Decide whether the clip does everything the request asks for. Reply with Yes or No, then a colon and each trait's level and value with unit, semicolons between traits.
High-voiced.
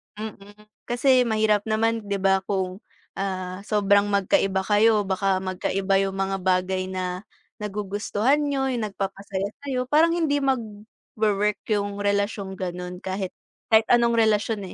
Yes: high, 205 Hz